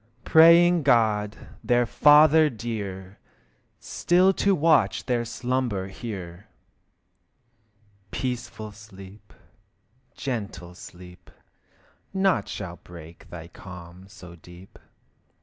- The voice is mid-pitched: No, low, 105 Hz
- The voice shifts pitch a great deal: Yes, wide, 6.0 semitones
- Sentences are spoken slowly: Yes, slow, 85 wpm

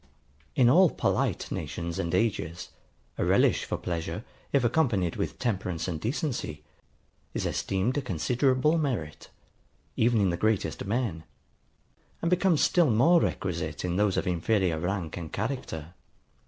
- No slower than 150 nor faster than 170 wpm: No, average, 140 wpm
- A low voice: Yes, low, 100 Hz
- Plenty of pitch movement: Yes, wide, 7.1 semitones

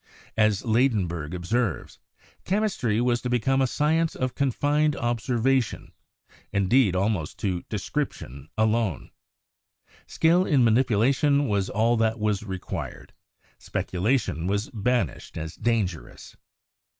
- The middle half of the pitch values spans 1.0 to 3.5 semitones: No, average, 4.9 semitones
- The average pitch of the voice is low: Yes, low, 115 Hz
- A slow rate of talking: Yes, slow, 115 wpm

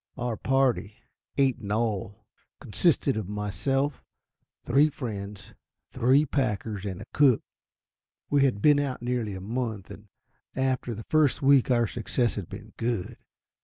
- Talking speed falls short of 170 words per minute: Yes, average, 140 wpm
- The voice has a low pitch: Yes, low, 120 Hz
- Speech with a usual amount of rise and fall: Yes, average, 4.4 semitones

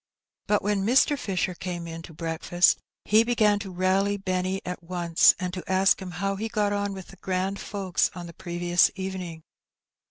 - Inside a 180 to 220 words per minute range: Yes, average, 185 wpm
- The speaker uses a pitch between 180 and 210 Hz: Yes, medium, 185 Hz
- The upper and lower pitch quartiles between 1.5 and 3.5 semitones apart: Yes, narrow, 2.4 semitones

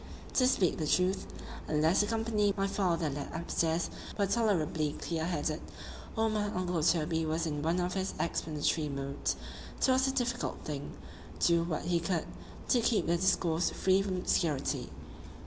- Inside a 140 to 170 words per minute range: Yes, average, 165 wpm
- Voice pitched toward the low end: No, medium, 175 Hz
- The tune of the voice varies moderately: Yes, average, 4.0 semitones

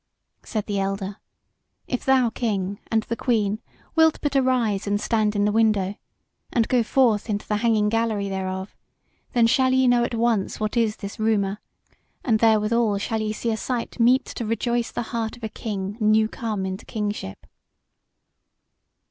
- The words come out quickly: No, average, 170 wpm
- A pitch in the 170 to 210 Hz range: No, high, 220 Hz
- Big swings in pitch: No, narrow, 2.4 semitones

